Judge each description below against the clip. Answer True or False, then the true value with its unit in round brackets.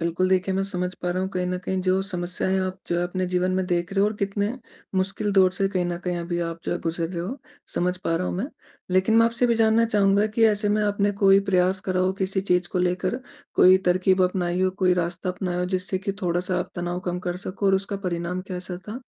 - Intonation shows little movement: True (1.7 semitones)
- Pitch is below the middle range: False (185 Hz)